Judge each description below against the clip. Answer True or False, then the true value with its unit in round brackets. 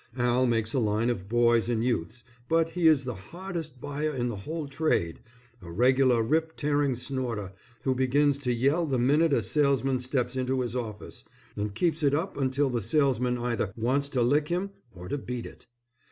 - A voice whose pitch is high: False (130 Hz)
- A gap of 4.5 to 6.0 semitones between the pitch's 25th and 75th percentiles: False (3.5 semitones)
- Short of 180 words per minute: False (190 wpm)